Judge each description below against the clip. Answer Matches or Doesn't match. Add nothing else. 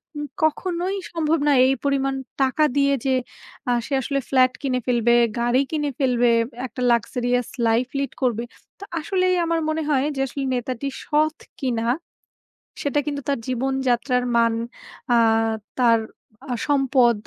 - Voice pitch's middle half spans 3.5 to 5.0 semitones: Doesn't match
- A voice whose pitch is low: Doesn't match